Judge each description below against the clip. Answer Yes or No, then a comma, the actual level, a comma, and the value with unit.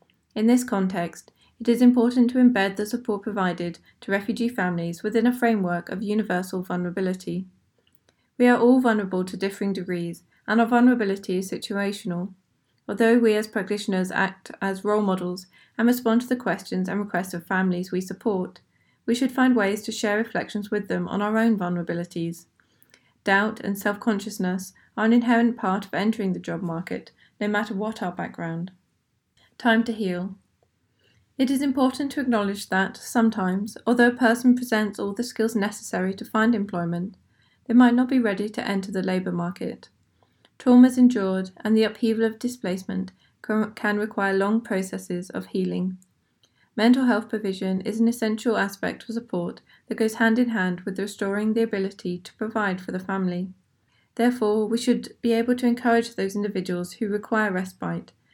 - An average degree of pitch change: Yes, average, 3.6 semitones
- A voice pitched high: Yes, high, 210 Hz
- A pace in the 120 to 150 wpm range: No, average, 165 wpm